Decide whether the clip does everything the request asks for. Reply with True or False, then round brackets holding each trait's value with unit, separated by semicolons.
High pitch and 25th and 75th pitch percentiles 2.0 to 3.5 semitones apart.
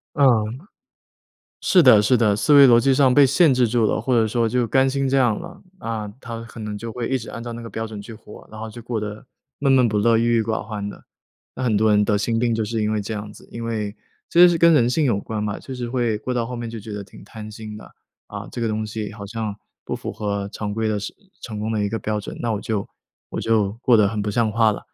False (115 Hz; 2.4 semitones)